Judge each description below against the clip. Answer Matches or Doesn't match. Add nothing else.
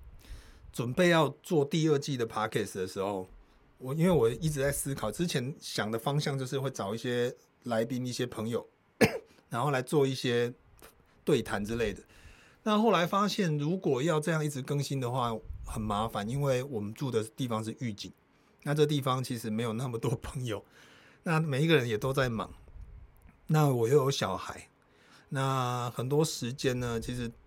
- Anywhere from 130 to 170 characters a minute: Doesn't match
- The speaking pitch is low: Matches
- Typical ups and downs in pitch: Matches